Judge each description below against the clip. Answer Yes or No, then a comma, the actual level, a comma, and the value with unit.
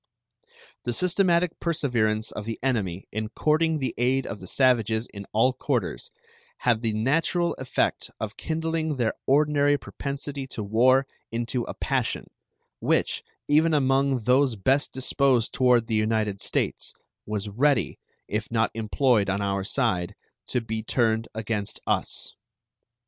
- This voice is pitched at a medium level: No, low, 120 Hz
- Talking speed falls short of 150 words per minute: Yes, average, 140 wpm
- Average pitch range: Yes, average, 4.3 semitones